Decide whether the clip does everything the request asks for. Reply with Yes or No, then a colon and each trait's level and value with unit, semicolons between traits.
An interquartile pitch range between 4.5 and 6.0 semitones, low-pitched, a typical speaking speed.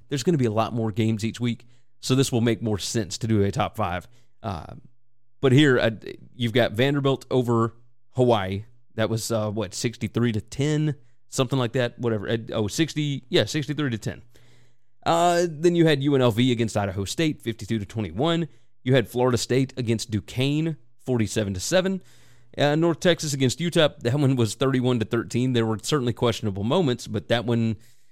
No: average, 3.1 semitones; low, 120 Hz; average, 185 wpm